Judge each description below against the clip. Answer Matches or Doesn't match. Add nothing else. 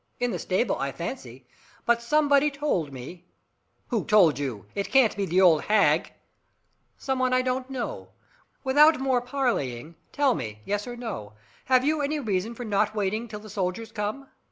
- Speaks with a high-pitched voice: Matches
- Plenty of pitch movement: Matches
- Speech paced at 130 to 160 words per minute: Doesn't match